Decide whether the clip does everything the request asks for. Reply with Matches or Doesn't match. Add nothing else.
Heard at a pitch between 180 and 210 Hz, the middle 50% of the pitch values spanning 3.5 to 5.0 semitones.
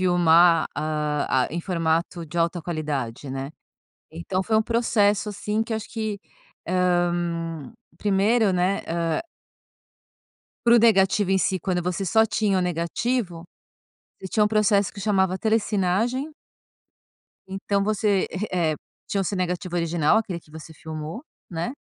Matches